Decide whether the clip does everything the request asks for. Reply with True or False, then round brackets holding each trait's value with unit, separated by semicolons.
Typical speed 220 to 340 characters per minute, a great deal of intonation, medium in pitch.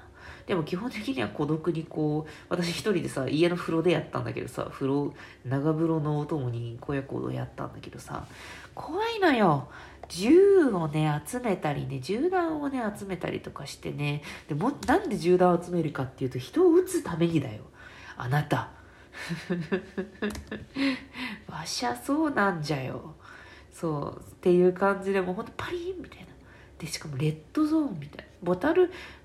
True (320 characters per minute; 6.6 semitones; 175 Hz)